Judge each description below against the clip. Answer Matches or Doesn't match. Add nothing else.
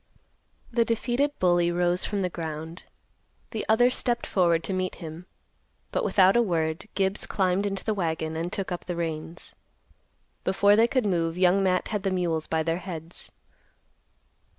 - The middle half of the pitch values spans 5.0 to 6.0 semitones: Doesn't match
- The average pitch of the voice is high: Doesn't match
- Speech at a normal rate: Matches